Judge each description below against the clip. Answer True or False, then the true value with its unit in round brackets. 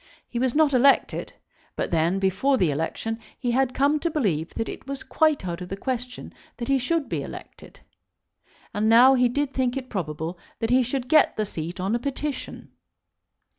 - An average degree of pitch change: False (6.0 semitones)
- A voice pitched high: True (245 Hz)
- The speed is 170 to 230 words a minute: True (190 wpm)